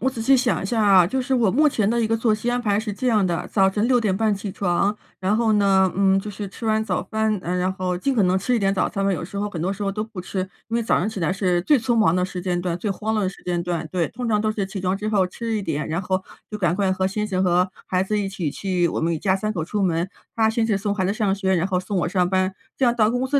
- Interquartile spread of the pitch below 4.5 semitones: Yes, average, 3.0 semitones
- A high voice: Yes, high, 195 Hz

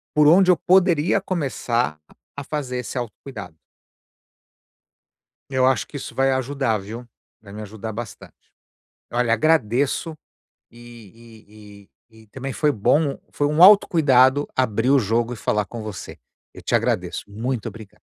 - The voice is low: Yes, low, 125 Hz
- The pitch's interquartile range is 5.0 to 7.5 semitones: No, average, 4.6 semitones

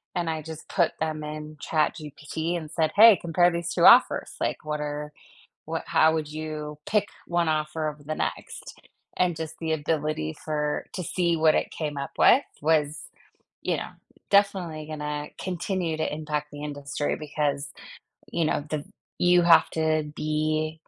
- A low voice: No, medium, 155 Hz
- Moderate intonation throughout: No, narrow, 1.8 semitones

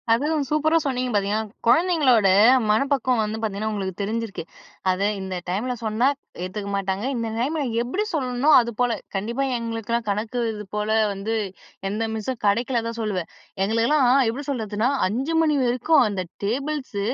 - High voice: Yes, high, 230 Hz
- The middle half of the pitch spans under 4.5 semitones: Yes, average, 3.7 semitones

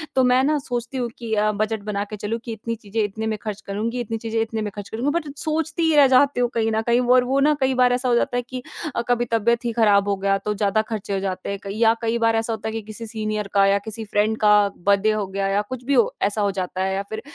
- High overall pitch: Yes, high, 220 Hz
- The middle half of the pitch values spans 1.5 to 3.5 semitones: Yes, average, 2.9 semitones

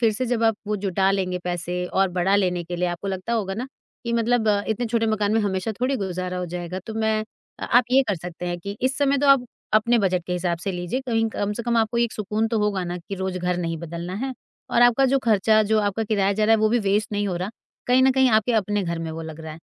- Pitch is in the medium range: No, high, 205 Hz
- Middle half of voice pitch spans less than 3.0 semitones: No, average, 4.0 semitones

